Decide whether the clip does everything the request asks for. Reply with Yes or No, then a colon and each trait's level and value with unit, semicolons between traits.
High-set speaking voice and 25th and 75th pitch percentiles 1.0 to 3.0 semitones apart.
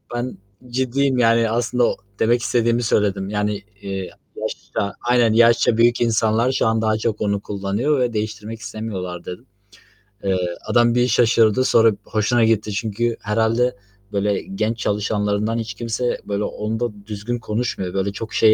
No: low, 110 Hz; narrow, 2.4 semitones